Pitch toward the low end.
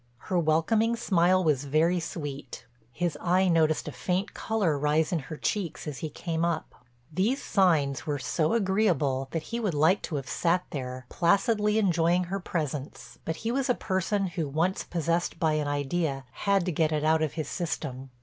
No: medium, 165 Hz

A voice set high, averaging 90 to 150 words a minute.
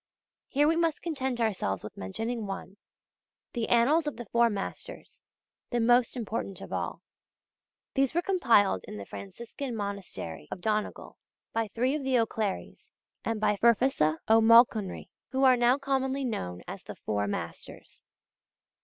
Yes: high, 230 Hz; average, 145 wpm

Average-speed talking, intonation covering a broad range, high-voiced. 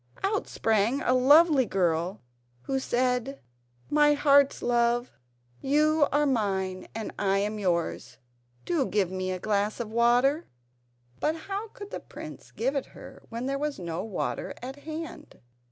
Yes: average, 150 wpm; wide, 6.2 semitones; high, 245 Hz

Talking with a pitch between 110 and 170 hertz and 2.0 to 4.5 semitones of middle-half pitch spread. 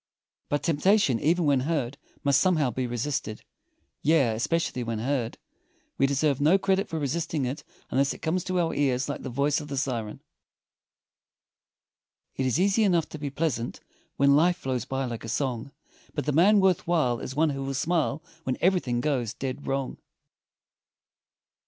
Yes: medium, 140 Hz; average, 4.1 semitones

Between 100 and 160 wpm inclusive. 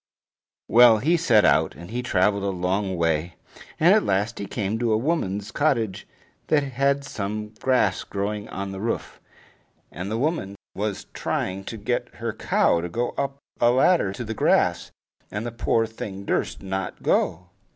No: average, 170 wpm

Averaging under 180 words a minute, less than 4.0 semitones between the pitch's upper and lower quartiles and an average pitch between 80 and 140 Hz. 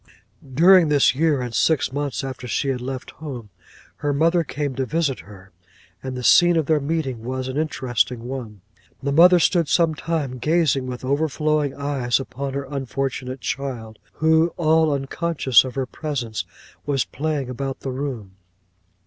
Yes: average, 160 wpm; average, 3.4 semitones; low, 135 Hz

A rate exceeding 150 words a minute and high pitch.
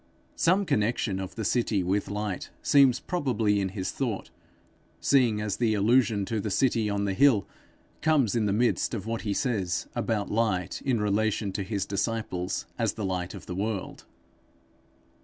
No: average, 165 wpm; low, 105 Hz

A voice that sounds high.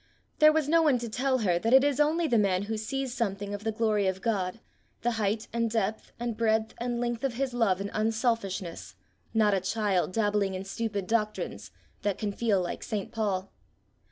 Yes: high, 220 Hz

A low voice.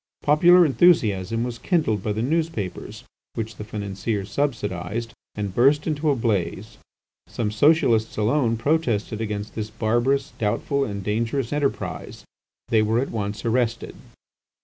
Yes: low, 115 Hz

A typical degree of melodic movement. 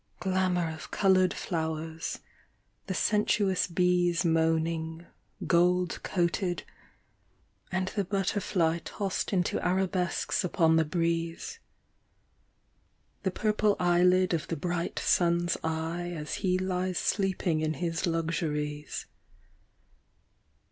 No: narrow, 2.3 semitones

